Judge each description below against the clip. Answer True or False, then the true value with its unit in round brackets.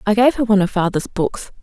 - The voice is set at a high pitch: True (210 Hz)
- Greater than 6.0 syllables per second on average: True (6.3 syllables/s)